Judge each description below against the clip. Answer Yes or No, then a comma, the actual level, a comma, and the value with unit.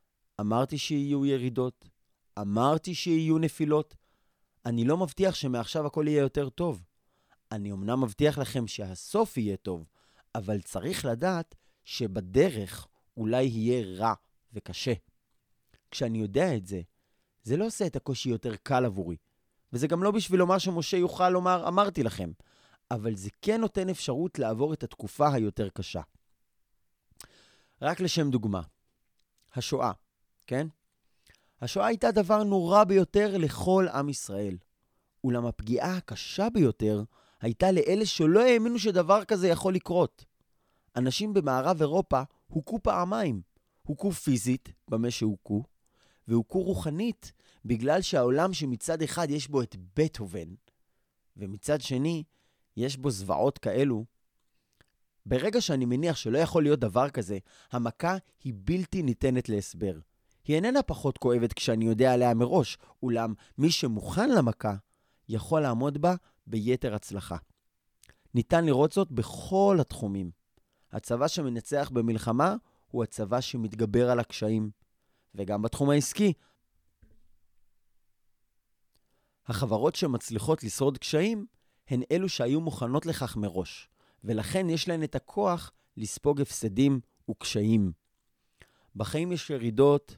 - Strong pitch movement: Yes, wide, 6.8 semitones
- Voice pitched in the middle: No, low, 130 Hz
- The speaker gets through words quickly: No, average, 120 wpm